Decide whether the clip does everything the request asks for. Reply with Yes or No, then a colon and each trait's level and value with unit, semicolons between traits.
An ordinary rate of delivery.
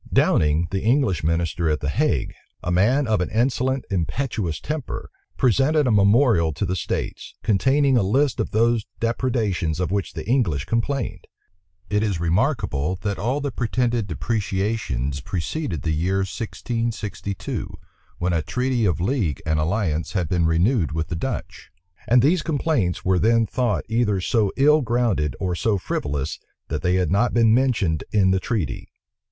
Yes: average, 160 wpm